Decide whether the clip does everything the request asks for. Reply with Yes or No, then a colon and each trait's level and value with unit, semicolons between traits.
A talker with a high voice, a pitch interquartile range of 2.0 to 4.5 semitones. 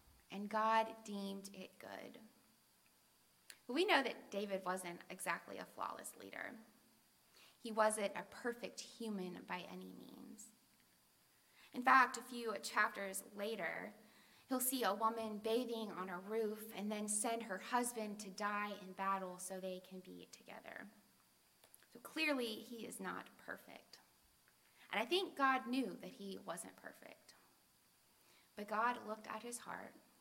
Yes: high, 220 Hz; average, 3.4 semitones